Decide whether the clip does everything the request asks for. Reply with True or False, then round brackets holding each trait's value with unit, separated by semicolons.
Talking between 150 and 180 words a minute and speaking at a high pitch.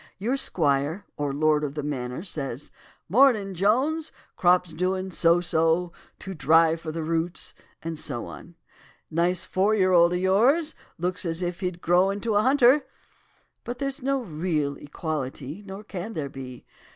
False (160 wpm; 175 Hz)